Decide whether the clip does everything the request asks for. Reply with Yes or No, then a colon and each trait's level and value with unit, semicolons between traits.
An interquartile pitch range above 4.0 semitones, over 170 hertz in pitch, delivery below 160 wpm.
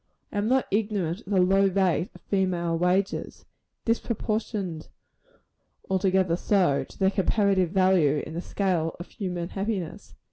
No: narrow, 2.5 semitones; high, 190 Hz; average, 140 wpm